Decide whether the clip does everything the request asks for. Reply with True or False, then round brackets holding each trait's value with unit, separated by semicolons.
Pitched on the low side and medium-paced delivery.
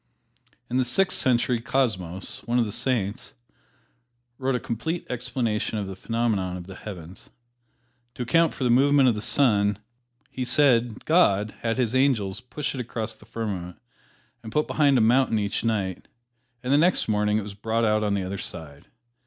True (115 Hz; 180 wpm)